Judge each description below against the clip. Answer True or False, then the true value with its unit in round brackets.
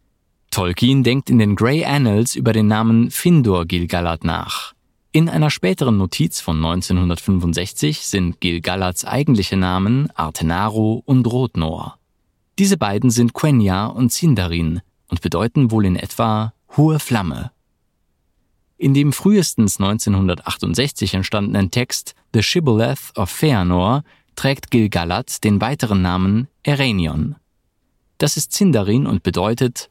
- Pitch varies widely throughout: True (6.2 semitones)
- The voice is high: False (110 Hz)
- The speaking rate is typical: False (120 wpm)